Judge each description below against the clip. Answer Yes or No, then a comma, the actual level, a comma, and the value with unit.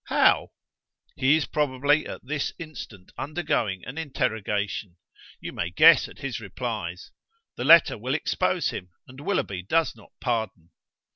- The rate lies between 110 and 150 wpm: Yes, average, 140 wpm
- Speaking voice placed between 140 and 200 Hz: No, low, 125 Hz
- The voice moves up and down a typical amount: No, wide, 6.7 semitones